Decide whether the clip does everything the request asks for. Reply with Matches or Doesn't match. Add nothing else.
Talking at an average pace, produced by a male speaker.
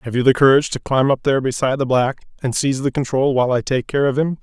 Doesn't match